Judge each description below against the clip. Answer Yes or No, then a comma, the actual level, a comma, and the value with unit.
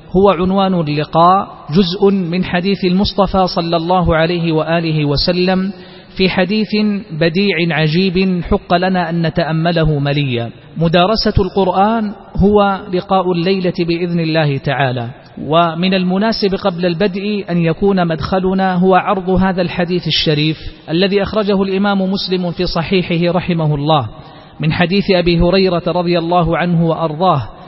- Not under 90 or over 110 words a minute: No, average, 125 wpm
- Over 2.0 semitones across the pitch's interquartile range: Yes, narrow, 2.5 semitones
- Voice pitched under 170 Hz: No, medium, 180 Hz